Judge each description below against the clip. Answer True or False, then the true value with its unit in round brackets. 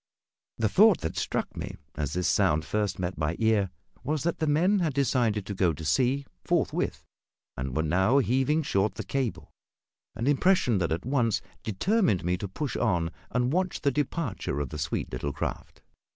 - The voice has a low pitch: True (110 Hz)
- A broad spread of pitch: True (8.2 semitones)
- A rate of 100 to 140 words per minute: False (180 wpm)